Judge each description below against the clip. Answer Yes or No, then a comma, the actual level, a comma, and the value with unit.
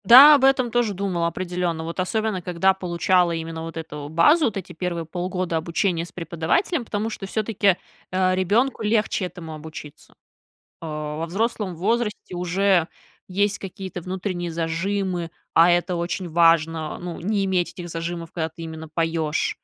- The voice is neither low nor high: Yes, medium, 180 Hz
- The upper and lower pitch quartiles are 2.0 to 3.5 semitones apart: Yes, average, 3.2 semitones